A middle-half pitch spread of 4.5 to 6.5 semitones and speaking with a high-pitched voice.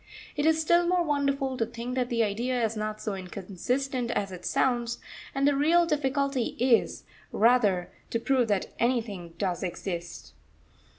Yes: average, 5.0 semitones; high, 240 Hz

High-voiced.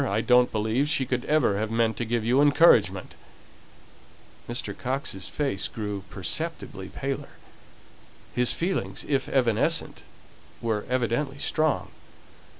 No: low, 120 Hz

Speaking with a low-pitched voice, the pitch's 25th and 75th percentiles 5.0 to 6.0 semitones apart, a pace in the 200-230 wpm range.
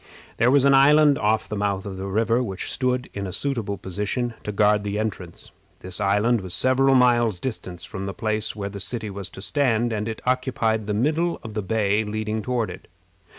No: low, 110 Hz; average, 3.7 semitones; fast, 205 wpm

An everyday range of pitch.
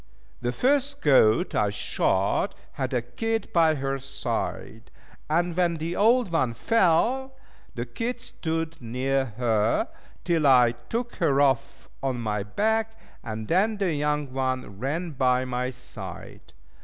No: wide, 6.8 semitones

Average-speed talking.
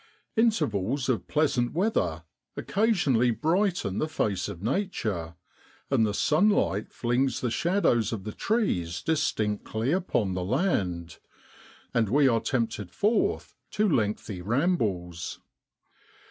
No: slow, 115 wpm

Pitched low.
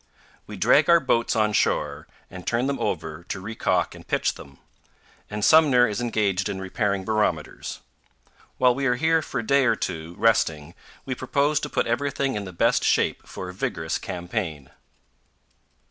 Yes: low, 110 Hz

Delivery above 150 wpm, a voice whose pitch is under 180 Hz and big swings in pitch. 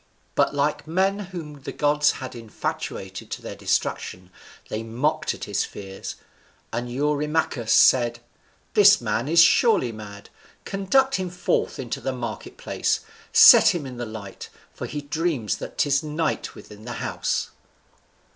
No: average, 145 wpm; medium, 140 Hz; wide, 5.9 semitones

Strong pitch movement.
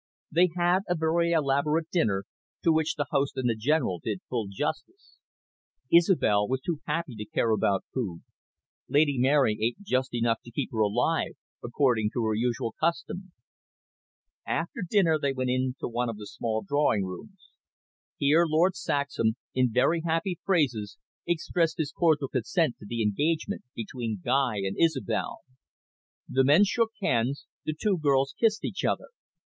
Yes: wide, 6.1 semitones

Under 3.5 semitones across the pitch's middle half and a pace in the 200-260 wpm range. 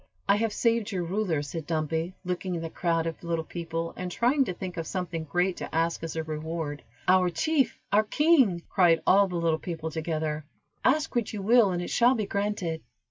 No: average, 3.8 semitones; fast, 205 wpm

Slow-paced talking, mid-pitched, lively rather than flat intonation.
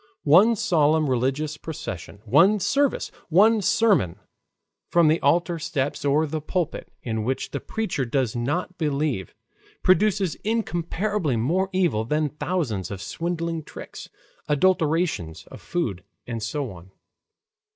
Yes: slow, 125 wpm; medium, 155 Hz; wide, 5.9 semitones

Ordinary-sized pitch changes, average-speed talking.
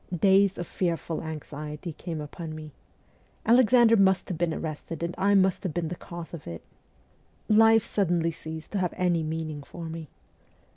Yes: average, 3.2 semitones; average, 165 wpm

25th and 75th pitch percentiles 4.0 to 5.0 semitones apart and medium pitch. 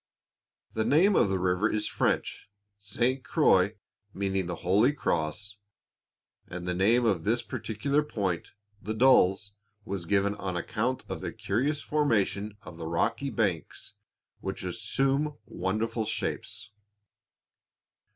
No: average, 4.3 semitones; low, 105 Hz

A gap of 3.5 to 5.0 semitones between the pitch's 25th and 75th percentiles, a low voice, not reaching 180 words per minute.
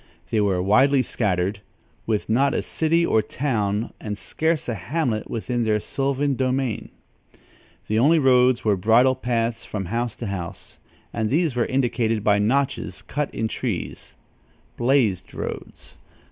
Yes: average, 4.0 semitones; low, 120 Hz; average, 145 wpm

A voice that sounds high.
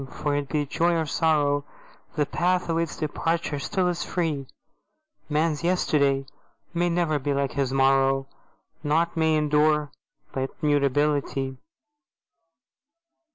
No: medium, 150 Hz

